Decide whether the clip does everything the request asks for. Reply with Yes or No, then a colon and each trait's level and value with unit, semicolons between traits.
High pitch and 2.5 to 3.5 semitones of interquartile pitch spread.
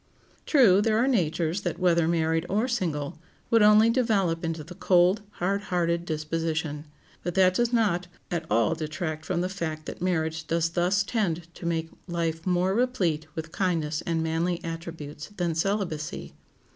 No: medium, 170 Hz; average, 3.0 semitones